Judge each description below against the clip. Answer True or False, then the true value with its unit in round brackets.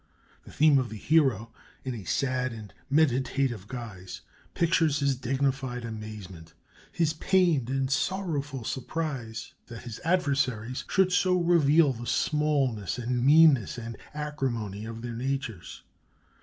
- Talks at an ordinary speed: False (130 wpm)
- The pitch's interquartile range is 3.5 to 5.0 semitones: True (4.6 semitones)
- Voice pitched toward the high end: False (130 Hz)